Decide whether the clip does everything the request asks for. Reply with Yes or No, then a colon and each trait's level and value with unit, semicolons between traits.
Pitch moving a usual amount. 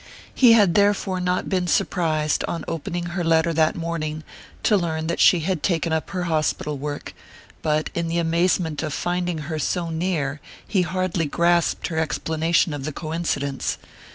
No: narrow, 2.3 semitones